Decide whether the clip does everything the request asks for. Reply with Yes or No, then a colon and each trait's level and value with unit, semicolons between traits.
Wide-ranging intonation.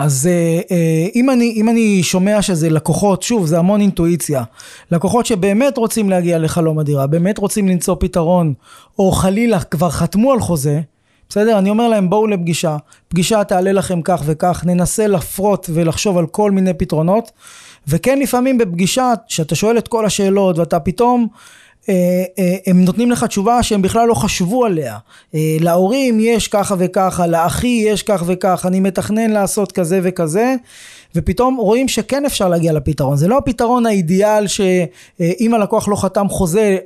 No: average, 4.0 semitones